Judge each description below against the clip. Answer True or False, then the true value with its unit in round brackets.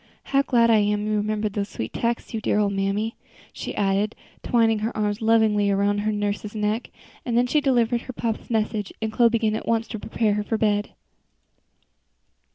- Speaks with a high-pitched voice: True (215 Hz)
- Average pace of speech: True (190 wpm)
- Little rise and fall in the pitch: True (1.8 semitones)